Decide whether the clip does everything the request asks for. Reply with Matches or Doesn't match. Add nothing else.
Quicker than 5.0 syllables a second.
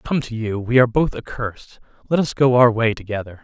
Matches